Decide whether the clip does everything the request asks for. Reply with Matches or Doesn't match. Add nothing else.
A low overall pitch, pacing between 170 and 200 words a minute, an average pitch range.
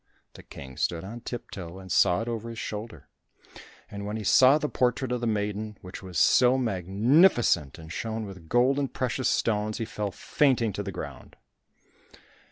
Matches